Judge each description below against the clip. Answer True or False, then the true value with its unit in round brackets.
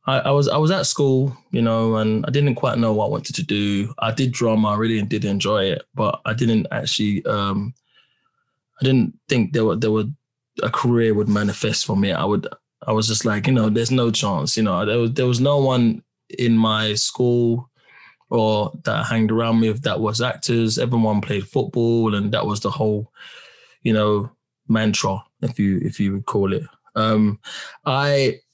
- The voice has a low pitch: True (115 Hz)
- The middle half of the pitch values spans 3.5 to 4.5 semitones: False (3.1 semitones)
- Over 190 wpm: True (200 wpm)